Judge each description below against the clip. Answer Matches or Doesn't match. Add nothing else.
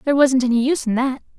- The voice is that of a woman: Matches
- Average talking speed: Doesn't match